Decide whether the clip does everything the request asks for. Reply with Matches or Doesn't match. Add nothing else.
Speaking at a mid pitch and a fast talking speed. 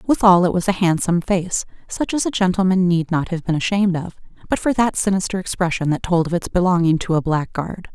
Matches